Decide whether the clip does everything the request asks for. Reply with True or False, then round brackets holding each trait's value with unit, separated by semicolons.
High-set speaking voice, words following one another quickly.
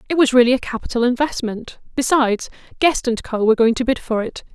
True (245 Hz; 210 wpm)